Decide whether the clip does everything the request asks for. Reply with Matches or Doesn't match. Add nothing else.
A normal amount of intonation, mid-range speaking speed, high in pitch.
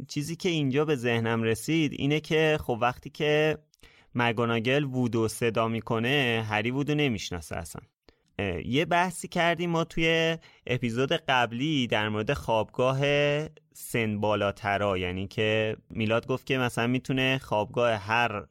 Doesn't match